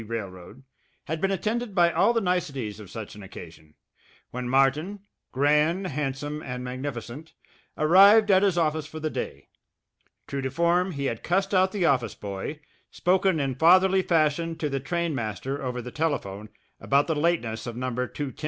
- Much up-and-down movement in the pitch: Yes, wide, 5.8 semitones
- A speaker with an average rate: Yes, average, 160 wpm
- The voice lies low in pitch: No, medium, 150 Hz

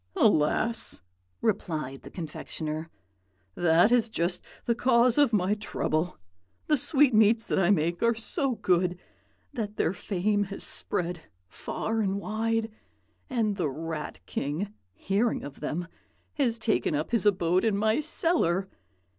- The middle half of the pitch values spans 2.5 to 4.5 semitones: No, average, 4.9 semitones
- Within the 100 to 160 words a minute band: Yes, slow, 135 wpm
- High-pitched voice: Yes, high, 200 Hz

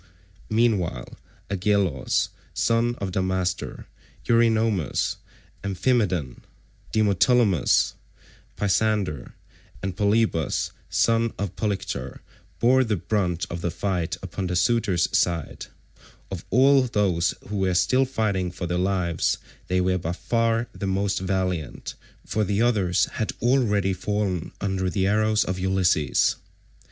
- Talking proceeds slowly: Yes, slow, 115 wpm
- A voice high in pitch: No, very low, 95 Hz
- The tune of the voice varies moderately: Yes, average, 3.5 semitones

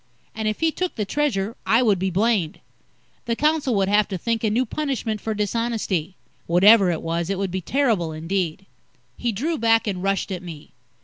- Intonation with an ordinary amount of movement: Yes, average, 3.8 semitones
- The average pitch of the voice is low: No, high, 210 Hz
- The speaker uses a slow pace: No, average, 195 wpm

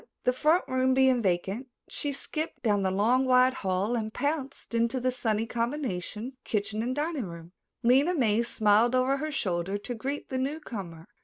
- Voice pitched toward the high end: Yes, high, 245 Hz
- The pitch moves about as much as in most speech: Yes, average, 4.2 semitones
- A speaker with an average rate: Yes, average, 170 wpm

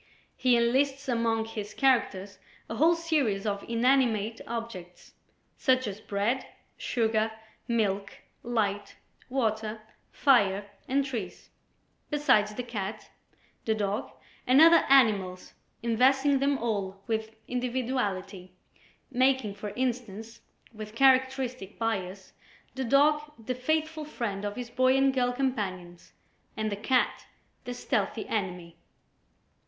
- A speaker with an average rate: No, slow, 115 wpm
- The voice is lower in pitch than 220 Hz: No, high, 230 Hz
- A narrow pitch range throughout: No, average, 4.1 semitones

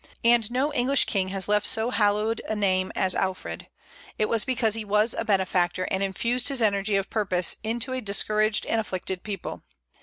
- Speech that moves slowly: No, average, 185 wpm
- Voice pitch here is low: No, high, 210 Hz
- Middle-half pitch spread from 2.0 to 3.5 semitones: Yes, average, 3.0 semitones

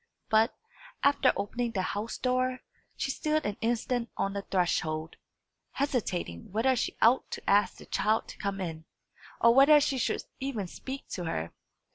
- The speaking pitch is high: Yes, high, 225 Hz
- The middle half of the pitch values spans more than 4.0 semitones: Yes, average, 4.9 semitones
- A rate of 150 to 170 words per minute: Yes, average, 160 wpm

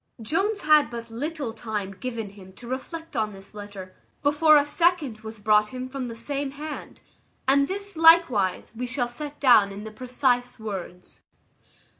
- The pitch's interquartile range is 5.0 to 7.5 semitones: Yes, wide, 5.4 semitones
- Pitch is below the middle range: No, high, 245 Hz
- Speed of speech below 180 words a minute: Yes, average, 165 wpm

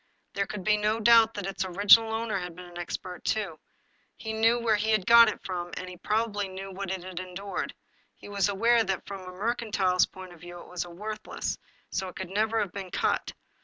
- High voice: Yes, high, 195 Hz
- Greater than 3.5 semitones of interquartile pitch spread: No, average, 3.0 semitones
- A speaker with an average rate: No, fast, 210 wpm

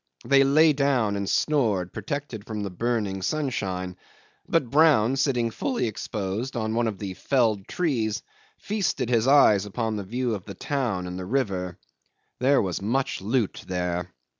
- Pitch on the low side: Yes, low, 115 Hz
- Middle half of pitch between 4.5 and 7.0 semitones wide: Yes, wide, 5.6 semitones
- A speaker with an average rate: Yes, average, 160 wpm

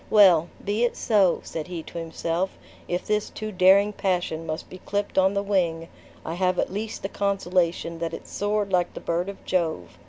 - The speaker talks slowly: No, average, 195 wpm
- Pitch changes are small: No, average, 3.2 semitones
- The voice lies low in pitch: No, medium, 185 Hz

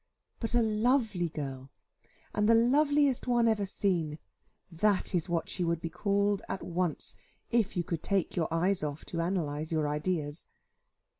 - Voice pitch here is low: No, medium, 185 Hz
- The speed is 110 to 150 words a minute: No, average, 160 wpm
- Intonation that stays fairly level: No, average, 5.0 semitones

